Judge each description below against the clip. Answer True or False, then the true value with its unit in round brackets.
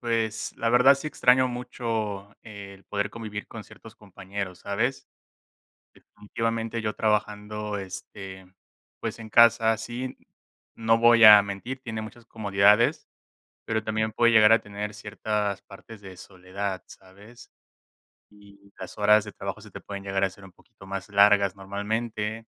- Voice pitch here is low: True (105 Hz)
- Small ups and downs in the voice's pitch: True (2.3 semitones)